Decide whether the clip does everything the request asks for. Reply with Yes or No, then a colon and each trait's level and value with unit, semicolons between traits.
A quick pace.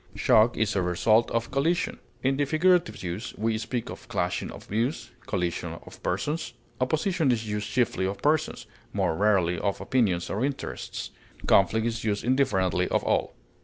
No: average, 165 wpm